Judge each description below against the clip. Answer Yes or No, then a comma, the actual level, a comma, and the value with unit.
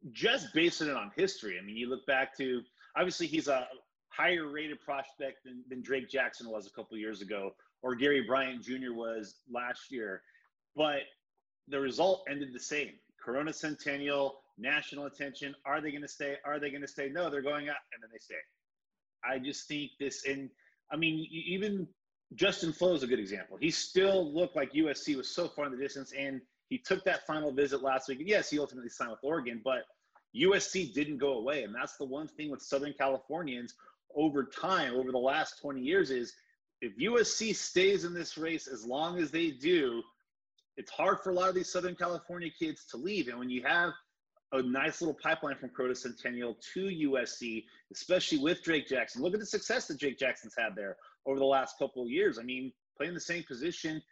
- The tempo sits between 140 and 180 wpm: No, fast, 205 wpm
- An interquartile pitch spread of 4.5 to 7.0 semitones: Yes, average, 5.3 semitones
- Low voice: No, medium, 145 Hz